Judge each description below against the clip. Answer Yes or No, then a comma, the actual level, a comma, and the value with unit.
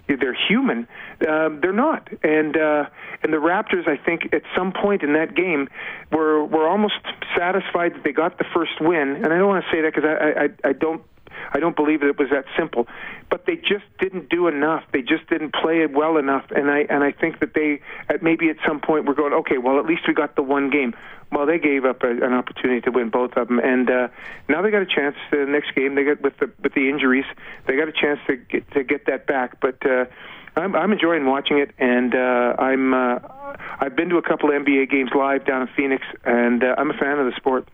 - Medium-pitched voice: Yes, medium, 150 Hz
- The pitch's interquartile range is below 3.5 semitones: Yes, average, 3.1 semitones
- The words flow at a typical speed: No, fast, 245 wpm